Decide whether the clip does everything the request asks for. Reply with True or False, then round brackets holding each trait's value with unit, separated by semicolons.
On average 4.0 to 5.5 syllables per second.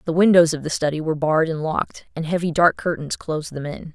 False (6.4 syllables/s)